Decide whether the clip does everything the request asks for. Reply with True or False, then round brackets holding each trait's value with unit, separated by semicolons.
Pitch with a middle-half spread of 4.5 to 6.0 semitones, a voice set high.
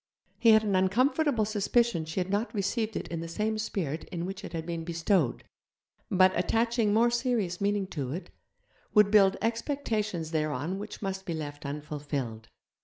True (4.9 semitones; 195 Hz)